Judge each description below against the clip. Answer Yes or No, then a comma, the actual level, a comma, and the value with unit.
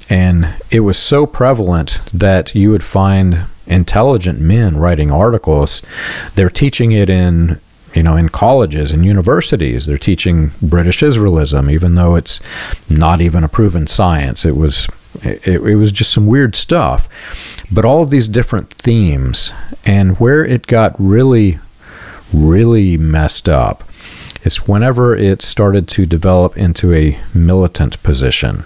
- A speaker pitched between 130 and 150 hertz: No, very low, 90 Hz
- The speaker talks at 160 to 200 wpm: No, average, 145 wpm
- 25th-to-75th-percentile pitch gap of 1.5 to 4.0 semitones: No, average, 4.9 semitones